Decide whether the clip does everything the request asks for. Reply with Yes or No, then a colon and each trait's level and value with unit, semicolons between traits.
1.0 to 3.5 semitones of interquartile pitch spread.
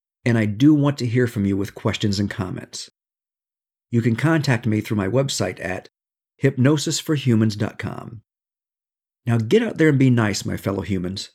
No: average, 4.9 semitones